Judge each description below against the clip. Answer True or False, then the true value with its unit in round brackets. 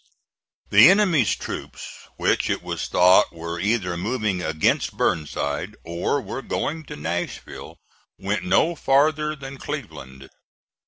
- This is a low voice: True (105 Hz)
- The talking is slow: True (120 wpm)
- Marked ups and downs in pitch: True (9.0 semitones)